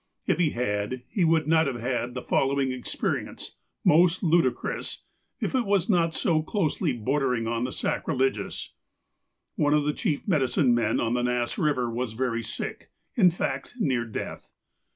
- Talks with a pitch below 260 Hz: Yes, low, 135 Hz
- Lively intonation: No, average, 4.9 semitones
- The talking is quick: No, average, 165 wpm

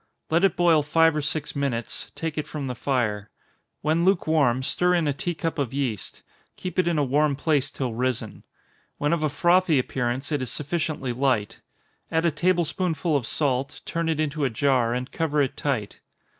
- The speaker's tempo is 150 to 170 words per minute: No, average, 195 wpm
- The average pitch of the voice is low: No, medium, 145 Hz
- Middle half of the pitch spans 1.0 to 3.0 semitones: No, average, 4.0 semitones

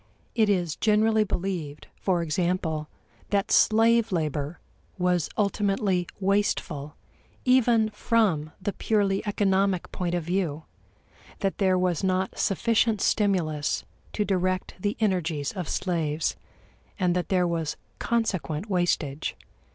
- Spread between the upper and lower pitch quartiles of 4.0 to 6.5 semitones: No, average, 3.5 semitones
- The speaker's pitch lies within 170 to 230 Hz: Yes, medium, 185 Hz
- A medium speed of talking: No, slow, 115 wpm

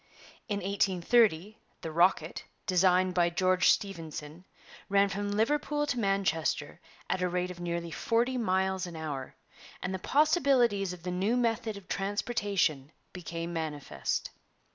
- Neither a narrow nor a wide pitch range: Yes, average, 3.3 semitones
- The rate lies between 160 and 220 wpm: No, slow, 135 wpm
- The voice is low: No, medium, 185 Hz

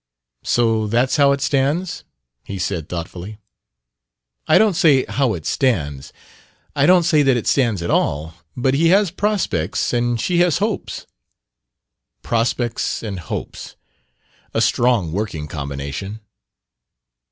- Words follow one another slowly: Yes, slow, 130 wpm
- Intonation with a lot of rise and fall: Yes, wide, 8.1 semitones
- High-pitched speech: No, low, 120 Hz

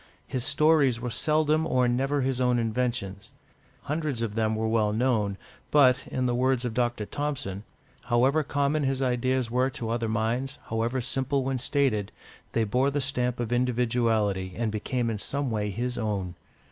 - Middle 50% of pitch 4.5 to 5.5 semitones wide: No, average, 3.0 semitones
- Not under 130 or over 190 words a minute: Yes, average, 170 wpm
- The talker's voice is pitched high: No, low, 125 Hz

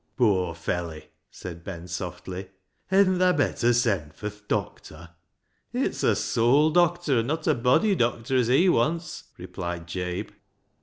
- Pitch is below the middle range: Yes, low, 115 Hz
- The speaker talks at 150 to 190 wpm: Yes, average, 165 wpm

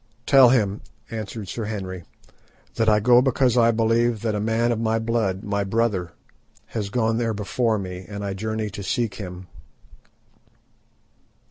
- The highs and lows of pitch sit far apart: No, narrow, 2.5 semitones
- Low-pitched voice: Yes, low, 110 Hz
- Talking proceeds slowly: No, average, 155 wpm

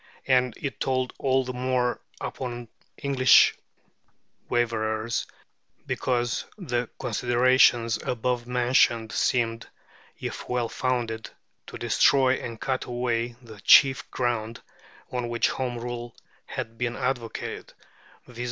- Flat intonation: Yes, narrow, 1.6 semitones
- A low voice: Yes, low, 120 Hz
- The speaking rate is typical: No, slow, 110 wpm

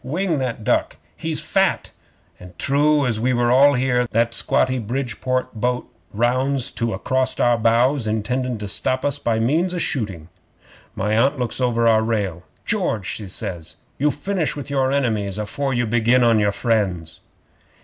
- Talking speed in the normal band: Yes, average, 160 wpm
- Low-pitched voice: Yes, low, 120 Hz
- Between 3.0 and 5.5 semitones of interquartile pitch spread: Yes, average, 3.3 semitones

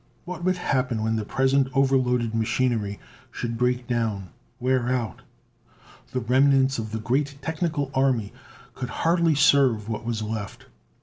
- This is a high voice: No, low, 125 Hz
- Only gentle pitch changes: No, average, 3.4 semitones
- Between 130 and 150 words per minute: Yes, average, 140 wpm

